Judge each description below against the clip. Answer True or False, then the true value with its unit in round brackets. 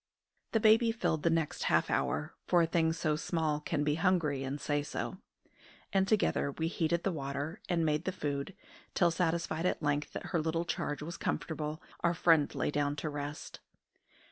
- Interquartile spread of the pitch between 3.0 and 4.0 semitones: False (2.6 semitones)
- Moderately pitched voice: True (160 Hz)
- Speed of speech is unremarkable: True (185 wpm)